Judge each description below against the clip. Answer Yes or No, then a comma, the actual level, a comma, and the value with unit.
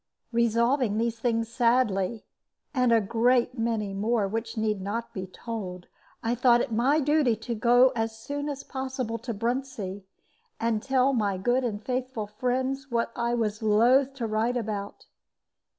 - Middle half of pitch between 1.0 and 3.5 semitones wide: Yes, average, 2.7 semitones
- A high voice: Yes, high, 235 Hz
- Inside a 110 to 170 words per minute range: Yes, average, 155 wpm